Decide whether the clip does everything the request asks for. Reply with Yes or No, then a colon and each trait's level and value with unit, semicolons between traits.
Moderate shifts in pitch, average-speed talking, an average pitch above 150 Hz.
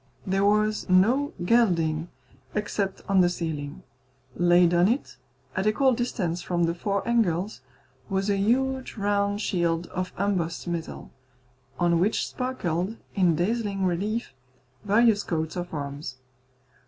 No: average, 3.7 semitones; slow, 130 wpm; high, 190 Hz